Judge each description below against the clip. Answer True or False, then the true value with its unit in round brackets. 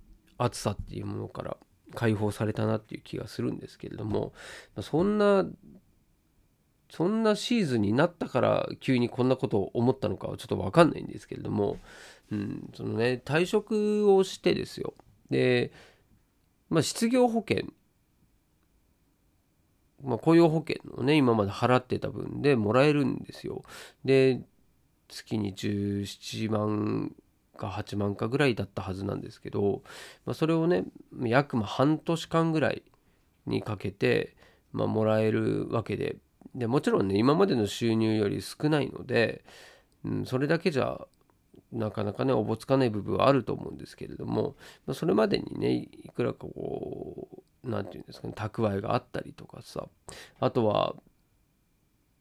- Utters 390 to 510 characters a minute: False (285 characters per minute)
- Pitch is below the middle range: True (120 Hz)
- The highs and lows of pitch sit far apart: True (6.2 semitones)